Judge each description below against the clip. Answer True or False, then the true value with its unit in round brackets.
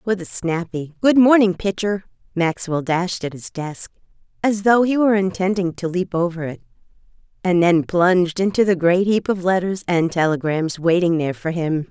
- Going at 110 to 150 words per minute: False (175 wpm)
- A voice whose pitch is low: False (180 Hz)